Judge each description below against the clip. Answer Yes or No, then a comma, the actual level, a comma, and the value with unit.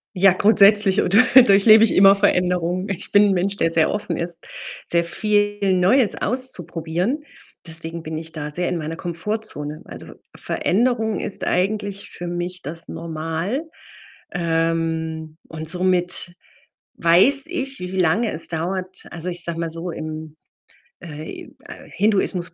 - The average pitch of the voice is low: No, medium, 180 Hz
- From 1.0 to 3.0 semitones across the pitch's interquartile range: No, average, 3.7 semitones